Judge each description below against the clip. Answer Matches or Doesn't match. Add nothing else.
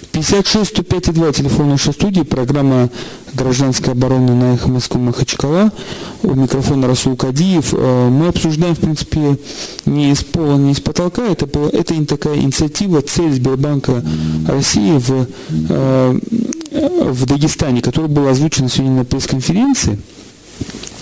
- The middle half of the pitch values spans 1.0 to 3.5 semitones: Doesn't match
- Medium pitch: Matches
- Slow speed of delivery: Doesn't match